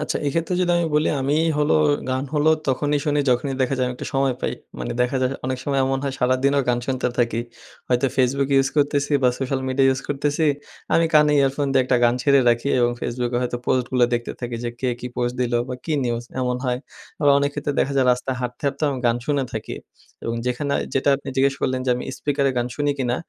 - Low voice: Yes, low, 130 Hz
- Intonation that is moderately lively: No, narrow, 2.3 semitones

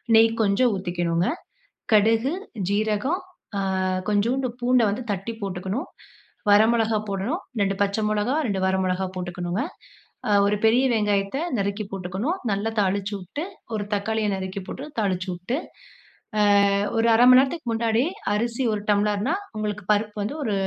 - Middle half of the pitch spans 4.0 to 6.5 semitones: No, average, 2.8 semitones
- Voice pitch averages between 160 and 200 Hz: No, high, 210 Hz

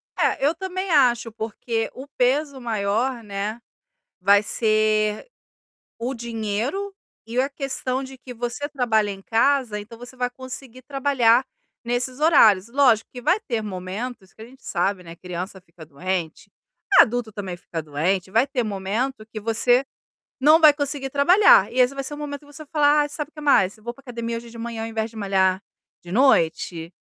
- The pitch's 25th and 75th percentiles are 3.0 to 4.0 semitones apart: No, average, 4.6 semitones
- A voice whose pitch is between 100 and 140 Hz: No, high, 235 Hz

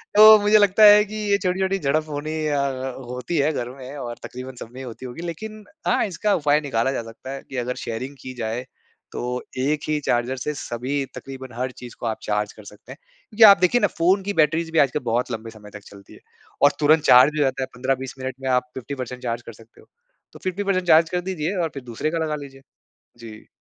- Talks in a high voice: No, low, 135 Hz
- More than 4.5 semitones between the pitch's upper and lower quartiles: Yes, average, 4.9 semitones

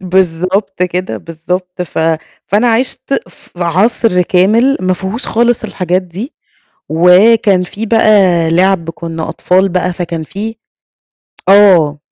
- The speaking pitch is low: No, medium, 185 Hz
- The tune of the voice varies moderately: Yes, average, 3.0 semitones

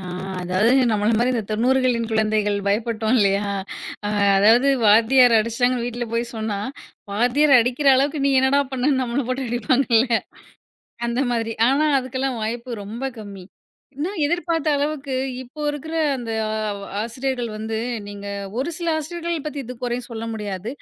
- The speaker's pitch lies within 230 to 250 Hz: Yes, high, 240 Hz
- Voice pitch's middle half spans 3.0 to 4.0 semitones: Yes, average, 3.5 semitones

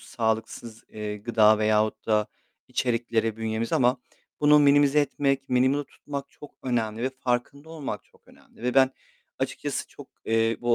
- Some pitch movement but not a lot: Yes, average, 3.6 semitones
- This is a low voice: Yes, low, 120 Hz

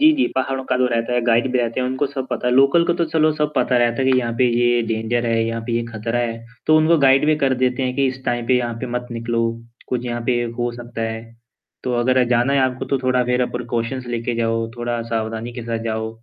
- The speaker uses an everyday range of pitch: No, narrow, 2.0 semitones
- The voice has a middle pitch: No, low, 120 Hz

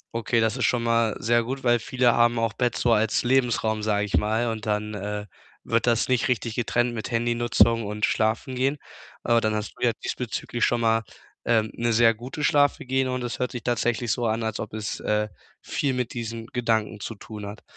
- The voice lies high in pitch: No, low, 115 Hz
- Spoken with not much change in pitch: Yes, narrow, 1.8 semitones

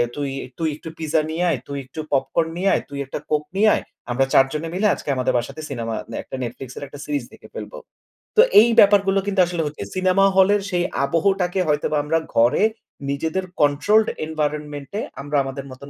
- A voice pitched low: No, medium, 155 Hz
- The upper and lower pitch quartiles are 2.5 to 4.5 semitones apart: No, average, 4.9 semitones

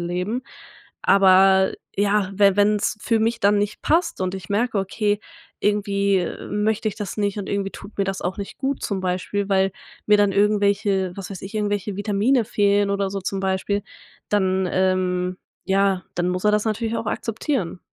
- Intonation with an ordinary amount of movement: No, narrow, 1.6 semitones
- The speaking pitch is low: No, high, 200 Hz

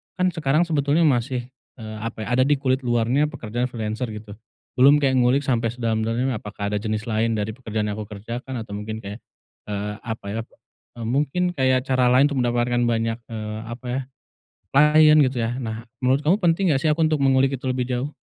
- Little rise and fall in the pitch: No, average, 3.7 semitones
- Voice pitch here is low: Yes, low, 125 Hz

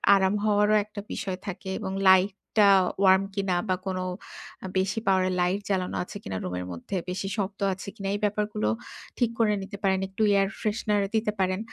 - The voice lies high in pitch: Yes, high, 195 Hz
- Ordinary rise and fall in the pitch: No, narrow, 1.7 semitones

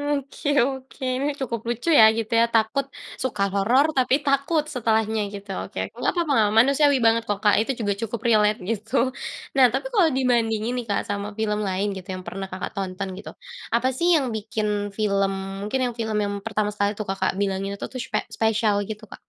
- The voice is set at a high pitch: Yes, high, 220 Hz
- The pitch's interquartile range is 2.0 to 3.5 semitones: No, average, 3.9 semitones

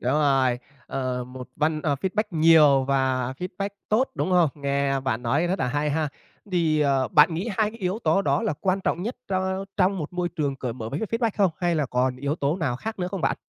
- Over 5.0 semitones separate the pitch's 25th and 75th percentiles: Yes, wide, 5.4 semitones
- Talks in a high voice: No, medium, 155 Hz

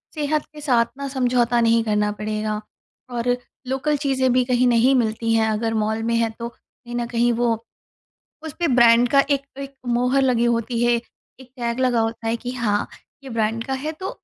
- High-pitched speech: Yes, high, 240 Hz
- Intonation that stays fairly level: Yes, narrow, 2.3 semitones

